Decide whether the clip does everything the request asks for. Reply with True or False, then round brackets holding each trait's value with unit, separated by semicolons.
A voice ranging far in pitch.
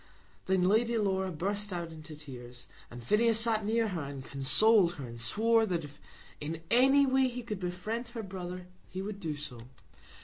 True (6.5 semitones)